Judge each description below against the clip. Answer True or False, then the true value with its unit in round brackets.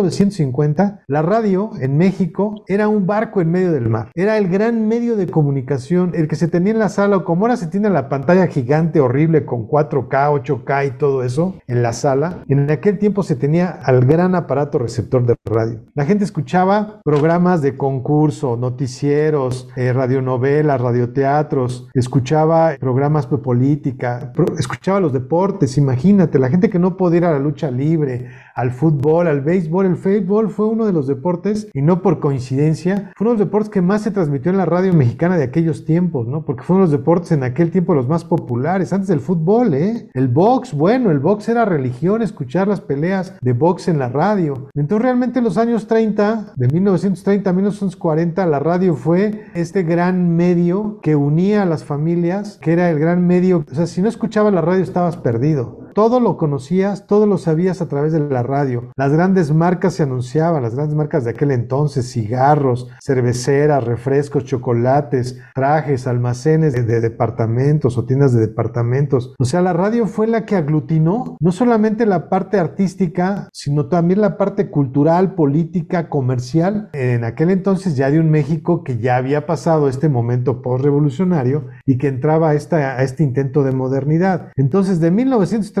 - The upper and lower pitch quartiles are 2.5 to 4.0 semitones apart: False (5.3 semitones)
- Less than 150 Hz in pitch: False (160 Hz)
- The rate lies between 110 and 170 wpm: False (185 wpm)